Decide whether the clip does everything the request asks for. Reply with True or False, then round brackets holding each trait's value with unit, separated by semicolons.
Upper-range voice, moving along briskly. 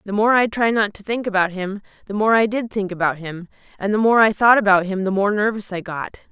True (205 Hz; 265 wpm)